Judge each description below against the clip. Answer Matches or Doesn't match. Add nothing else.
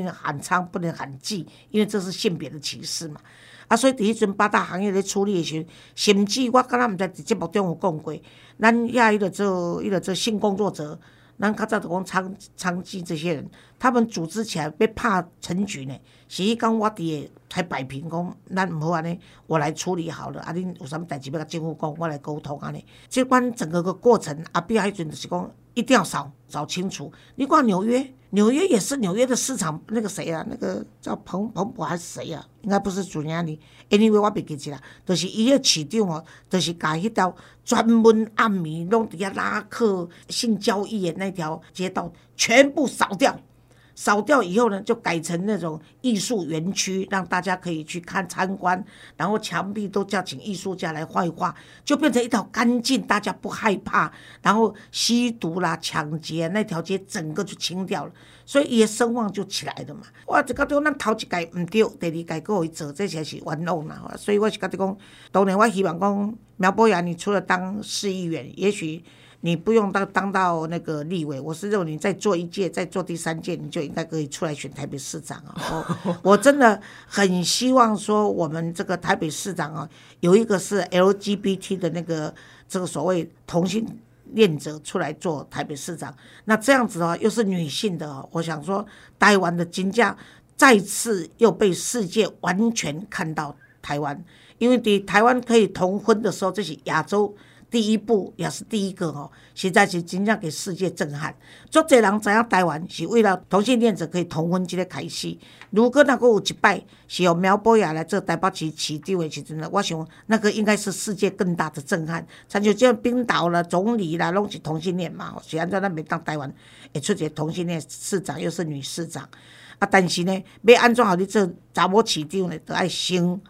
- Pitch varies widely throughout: Doesn't match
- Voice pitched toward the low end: Doesn't match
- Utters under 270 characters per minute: Doesn't match